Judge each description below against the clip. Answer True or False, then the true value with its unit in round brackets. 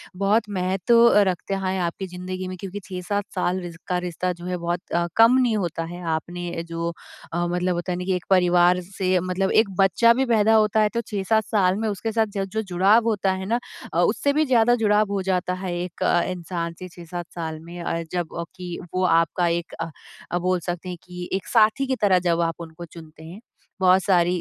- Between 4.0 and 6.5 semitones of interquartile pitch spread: False (2.8 semitones)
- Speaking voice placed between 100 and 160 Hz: False (185 Hz)